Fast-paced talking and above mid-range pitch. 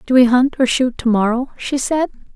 Yes: fast, 230 wpm; very high, 250 Hz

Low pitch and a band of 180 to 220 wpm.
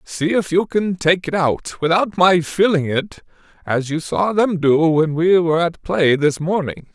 No: medium, 170 Hz; average, 200 wpm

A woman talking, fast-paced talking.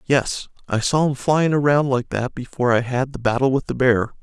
No: male; fast, 225 wpm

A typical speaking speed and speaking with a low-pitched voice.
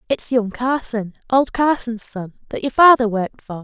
No: average, 180 wpm; high, 235 Hz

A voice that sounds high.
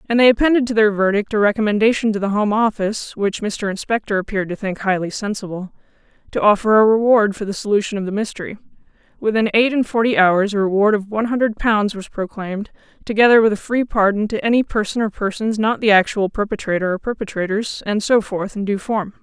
Yes: high, 210 Hz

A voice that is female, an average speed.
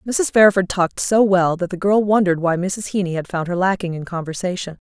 No: female; fast, 220 wpm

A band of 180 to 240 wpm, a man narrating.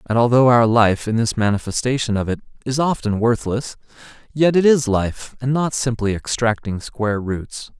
No: average, 170 wpm; male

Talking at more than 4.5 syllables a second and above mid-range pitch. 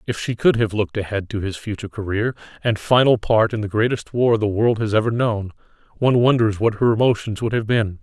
No: 5.9 syllables/s; low, 110 Hz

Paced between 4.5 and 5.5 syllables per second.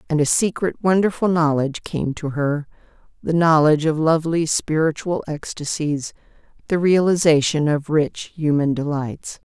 Yes: 4.7 syllables/s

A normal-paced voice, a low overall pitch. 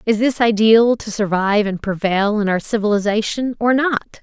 No: average, 170 wpm; high, 215 Hz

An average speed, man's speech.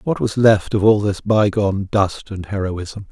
Yes: average, 195 wpm; male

